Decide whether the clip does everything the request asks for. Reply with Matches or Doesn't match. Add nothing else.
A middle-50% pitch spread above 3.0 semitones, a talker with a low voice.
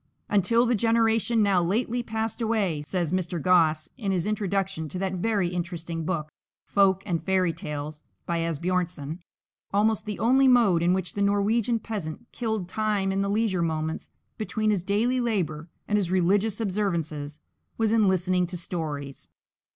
Doesn't match